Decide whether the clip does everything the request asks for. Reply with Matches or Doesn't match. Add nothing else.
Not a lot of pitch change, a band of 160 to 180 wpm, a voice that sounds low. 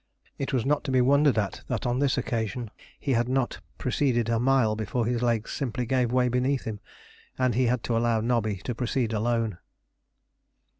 Doesn't match